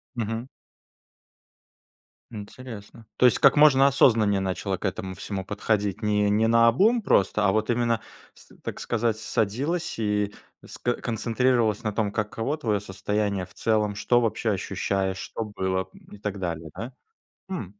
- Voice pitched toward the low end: Yes, low, 110 Hz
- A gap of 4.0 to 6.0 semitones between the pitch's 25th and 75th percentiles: No, average, 2.7 semitones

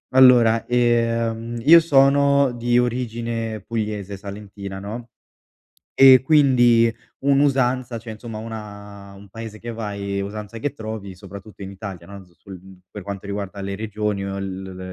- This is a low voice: Yes, low, 110 Hz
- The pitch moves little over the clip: No, average, 3.3 semitones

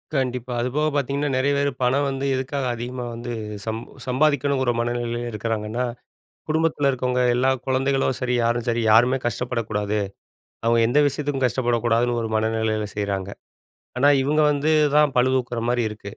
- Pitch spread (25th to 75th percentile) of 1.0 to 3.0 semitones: Yes, narrow, 2.6 semitones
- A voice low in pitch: Yes, low, 125 Hz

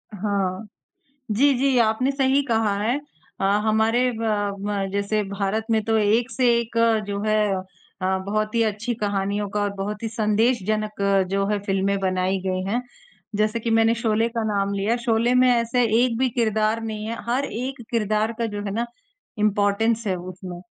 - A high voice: Yes, high, 215 Hz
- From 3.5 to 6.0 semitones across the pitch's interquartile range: No, narrow, 2.4 semitones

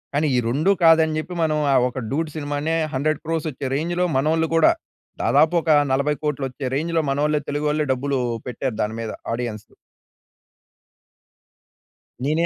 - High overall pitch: No, medium, 150 Hz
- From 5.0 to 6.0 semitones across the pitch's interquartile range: No, average, 2.9 semitones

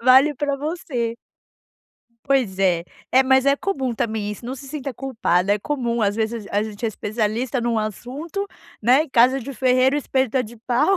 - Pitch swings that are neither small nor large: Yes, average, 3.7 semitones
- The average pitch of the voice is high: Yes, very high, 250 Hz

